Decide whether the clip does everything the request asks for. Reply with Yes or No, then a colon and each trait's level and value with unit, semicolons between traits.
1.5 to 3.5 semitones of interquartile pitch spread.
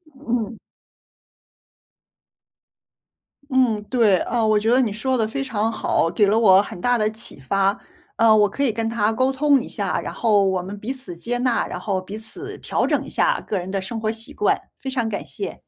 Yes: average, 3.2 semitones